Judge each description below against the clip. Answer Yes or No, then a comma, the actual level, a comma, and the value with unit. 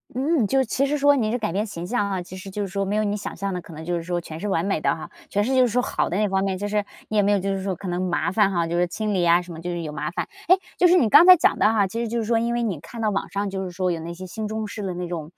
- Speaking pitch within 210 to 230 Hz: No, high, 200 Hz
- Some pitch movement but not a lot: Yes, average, 3.8 semitones